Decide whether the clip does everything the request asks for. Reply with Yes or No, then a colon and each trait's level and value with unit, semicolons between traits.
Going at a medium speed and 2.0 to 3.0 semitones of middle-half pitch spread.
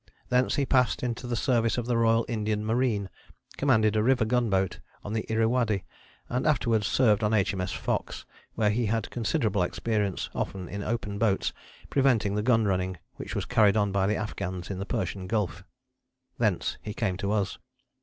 Yes: average, 175 wpm; average, 2.7 semitones